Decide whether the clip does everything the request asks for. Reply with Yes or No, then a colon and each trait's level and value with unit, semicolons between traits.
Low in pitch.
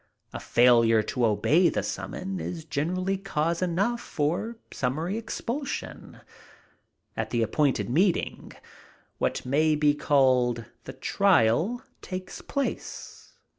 No: medium, 160 Hz